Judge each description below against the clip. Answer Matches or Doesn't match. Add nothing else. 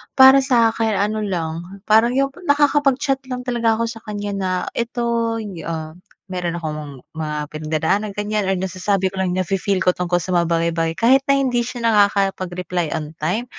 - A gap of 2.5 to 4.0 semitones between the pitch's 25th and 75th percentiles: Doesn't match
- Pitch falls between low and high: Doesn't match